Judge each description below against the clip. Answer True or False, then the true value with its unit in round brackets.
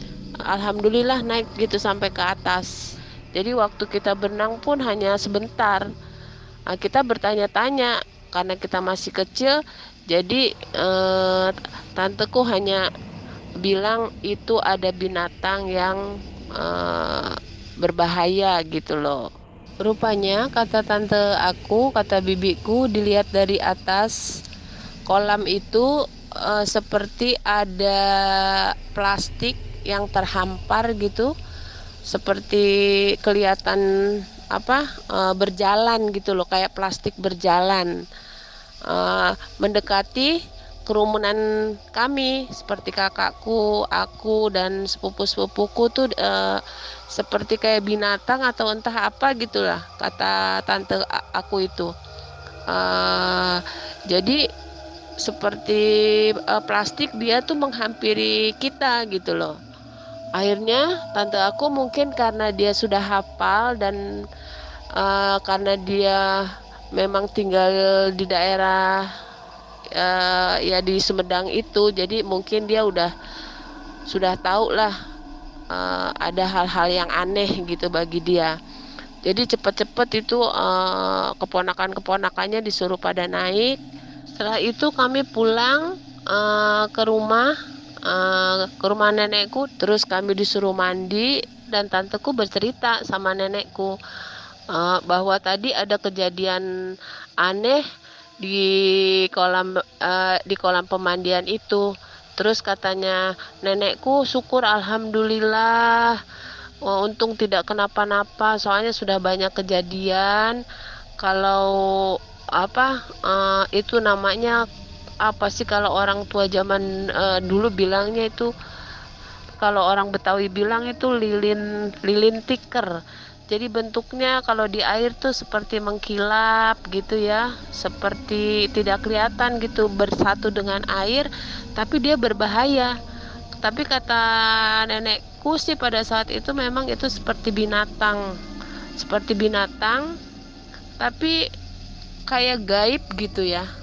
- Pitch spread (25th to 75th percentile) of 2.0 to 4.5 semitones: True (2.9 semitones)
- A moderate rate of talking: True (105 wpm)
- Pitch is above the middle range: True (205 Hz)